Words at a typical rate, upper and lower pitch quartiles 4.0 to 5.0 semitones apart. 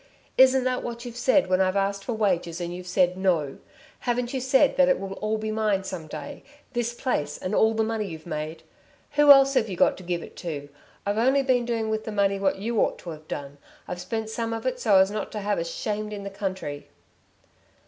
No: fast, 235 wpm; average, 4.6 semitones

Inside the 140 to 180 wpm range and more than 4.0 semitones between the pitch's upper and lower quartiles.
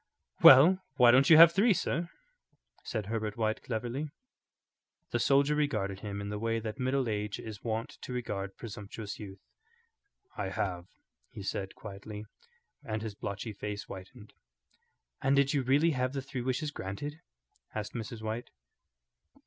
Yes: average, 150 wpm; average, 4.6 semitones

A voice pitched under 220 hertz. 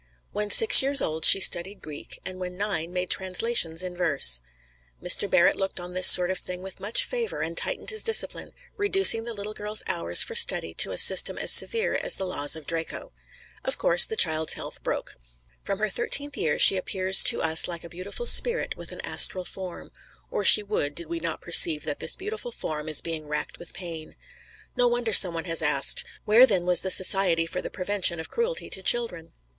Yes: medium, 185 Hz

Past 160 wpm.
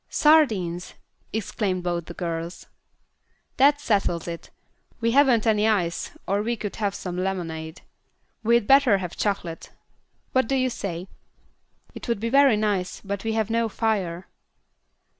No: average, 140 wpm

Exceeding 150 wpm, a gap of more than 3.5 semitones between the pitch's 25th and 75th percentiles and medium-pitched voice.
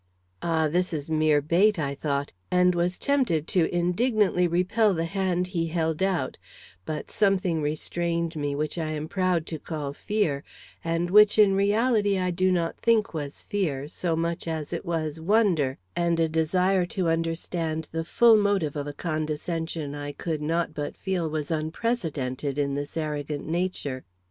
No: average, 170 wpm; average, 3.1 semitones; medium, 165 Hz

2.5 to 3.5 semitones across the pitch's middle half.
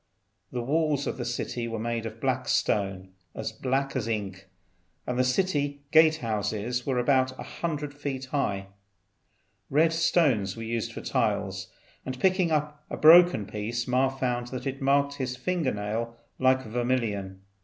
No: average, 4.1 semitones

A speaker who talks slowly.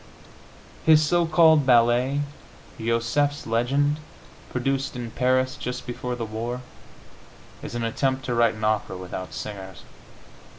Yes: slow, 125 wpm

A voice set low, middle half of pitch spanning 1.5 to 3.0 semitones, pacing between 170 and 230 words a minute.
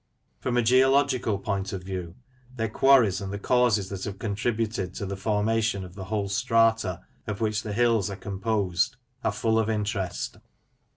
Yes: low, 105 Hz; narrow, 2.6 semitones; average, 175 wpm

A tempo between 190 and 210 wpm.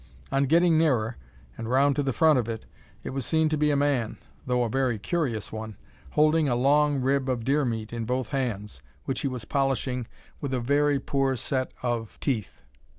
Yes: average, 200 wpm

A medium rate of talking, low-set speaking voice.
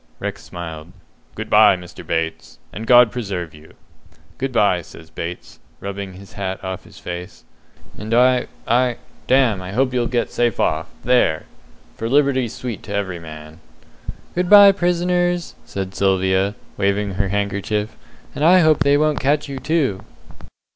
Yes: average, 155 wpm; low, 105 Hz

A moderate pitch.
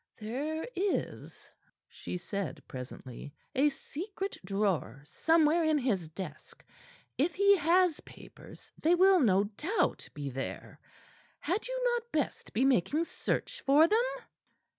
No: very high, 295 Hz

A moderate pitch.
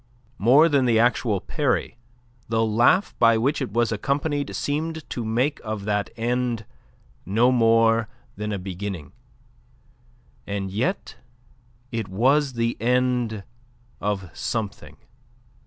No: low, 115 Hz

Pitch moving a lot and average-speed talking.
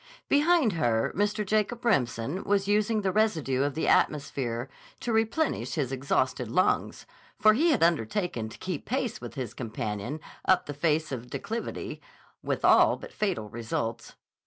Yes: wide, 9.0 semitones; average, 160 wpm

